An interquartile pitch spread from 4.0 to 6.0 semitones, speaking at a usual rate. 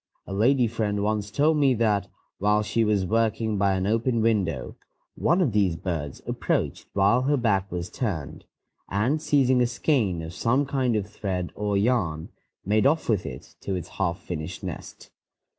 Yes: average, 4.3 semitones; average, 175 wpm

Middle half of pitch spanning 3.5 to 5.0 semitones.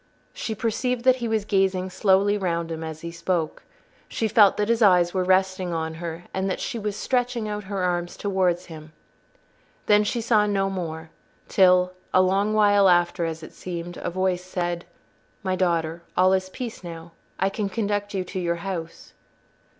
No: average, 2.9 semitones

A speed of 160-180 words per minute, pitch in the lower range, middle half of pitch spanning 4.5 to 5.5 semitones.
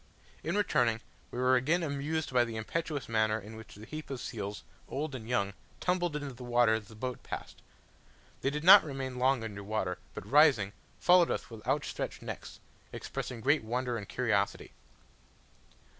Yes: average, 175 wpm; low, 125 Hz; average, 5.0 semitones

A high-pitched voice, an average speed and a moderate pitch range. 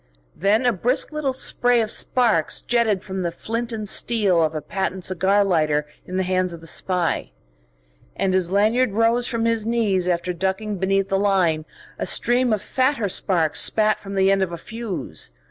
Yes: high, 195 Hz; average, 185 wpm; average, 3.9 semitones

